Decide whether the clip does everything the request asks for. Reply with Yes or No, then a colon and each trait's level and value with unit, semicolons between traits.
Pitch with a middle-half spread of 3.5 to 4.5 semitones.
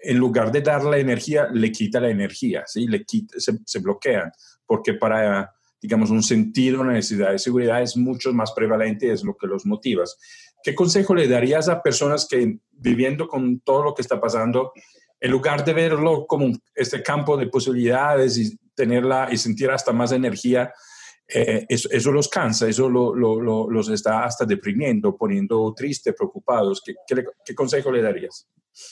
No: average, 5.2 semitones